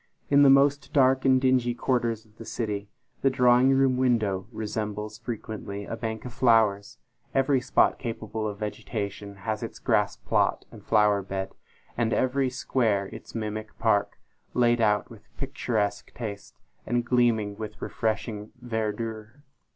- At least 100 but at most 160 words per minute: Yes, average, 145 wpm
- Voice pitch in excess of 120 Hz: No, low, 115 Hz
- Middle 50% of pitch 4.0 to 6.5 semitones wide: No, average, 3.1 semitones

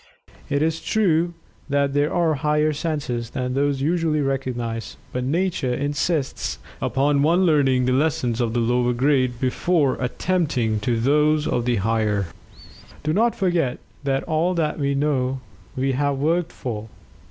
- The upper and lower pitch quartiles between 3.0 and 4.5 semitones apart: Yes, average, 3.7 semitones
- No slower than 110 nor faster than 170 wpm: Yes, average, 145 wpm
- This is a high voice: No, medium, 140 Hz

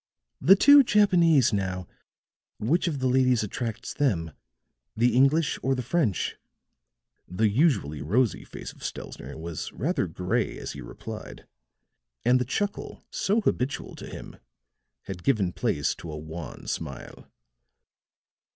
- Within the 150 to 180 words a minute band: No, slow, 135 wpm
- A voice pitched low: Yes, low, 125 Hz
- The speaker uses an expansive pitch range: Yes, wide, 8.3 semitones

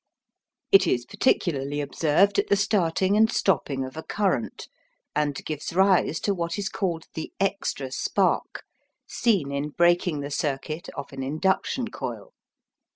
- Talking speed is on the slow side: No, average, 145 wpm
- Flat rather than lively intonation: No, wide, 5.4 semitones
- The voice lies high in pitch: No, medium, 165 Hz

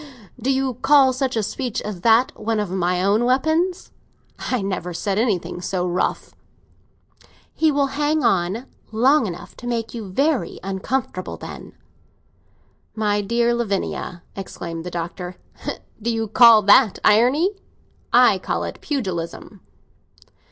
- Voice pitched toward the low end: No, high, 225 Hz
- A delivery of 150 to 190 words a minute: No, slow, 135 wpm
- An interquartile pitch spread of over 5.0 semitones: Yes, wide, 5.5 semitones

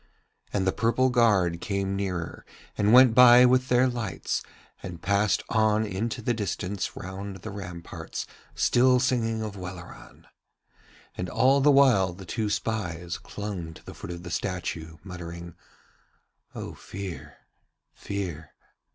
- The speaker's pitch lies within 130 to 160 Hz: No, low, 100 Hz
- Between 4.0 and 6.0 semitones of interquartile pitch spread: Yes, average, 4.4 semitones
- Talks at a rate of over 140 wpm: No, slow, 135 wpm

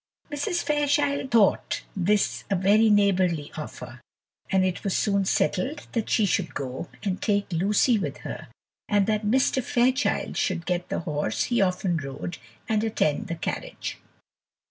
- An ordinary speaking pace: Yes, average, 150 wpm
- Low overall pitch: No, high, 200 Hz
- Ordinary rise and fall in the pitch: Yes, average, 4.2 semitones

